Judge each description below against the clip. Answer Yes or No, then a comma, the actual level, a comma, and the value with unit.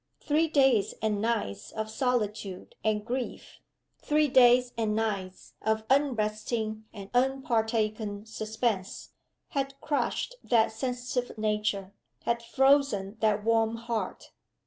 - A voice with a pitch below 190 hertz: No, high, 225 Hz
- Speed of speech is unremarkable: No, slow, 110 wpm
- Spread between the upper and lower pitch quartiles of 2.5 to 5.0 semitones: Yes, average, 2.8 semitones